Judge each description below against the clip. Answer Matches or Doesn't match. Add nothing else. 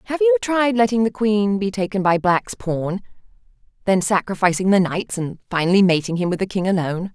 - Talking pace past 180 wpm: Matches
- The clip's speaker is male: Doesn't match